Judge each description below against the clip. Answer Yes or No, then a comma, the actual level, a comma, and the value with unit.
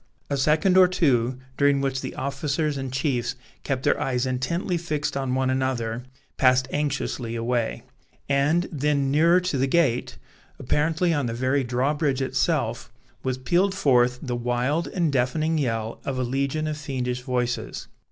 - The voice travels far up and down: No, average, 3.2 semitones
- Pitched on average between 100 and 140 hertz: Yes, low, 135 Hz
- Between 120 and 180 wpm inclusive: Yes, average, 155 wpm